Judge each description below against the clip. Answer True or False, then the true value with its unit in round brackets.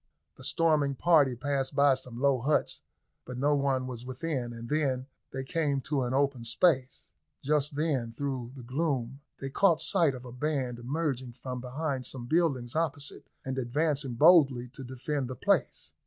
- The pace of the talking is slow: False (170 wpm)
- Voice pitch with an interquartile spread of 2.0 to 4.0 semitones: True (2.9 semitones)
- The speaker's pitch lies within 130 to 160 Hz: True (135 Hz)